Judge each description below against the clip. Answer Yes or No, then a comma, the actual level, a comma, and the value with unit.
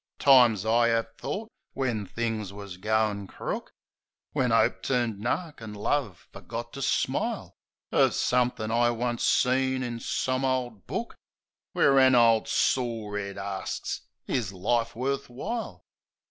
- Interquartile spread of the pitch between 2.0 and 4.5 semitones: Yes, average, 3.2 semitones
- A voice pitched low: Yes, low, 120 Hz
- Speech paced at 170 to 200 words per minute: No, slow, 135 wpm